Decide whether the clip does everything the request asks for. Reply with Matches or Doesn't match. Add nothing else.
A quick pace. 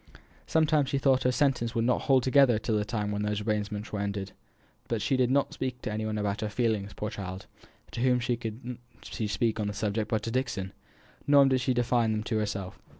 Matches